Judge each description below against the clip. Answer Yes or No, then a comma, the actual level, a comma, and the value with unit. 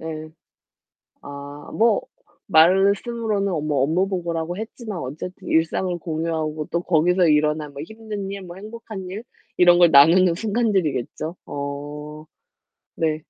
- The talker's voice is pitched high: No, medium, 170 Hz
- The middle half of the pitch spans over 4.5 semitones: No, average, 4.2 semitones